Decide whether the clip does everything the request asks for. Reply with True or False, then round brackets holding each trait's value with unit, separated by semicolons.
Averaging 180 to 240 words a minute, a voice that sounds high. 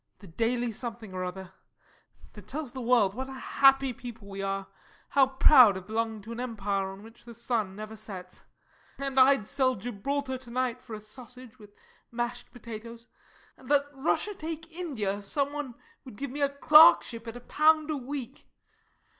True (185 wpm; 240 Hz)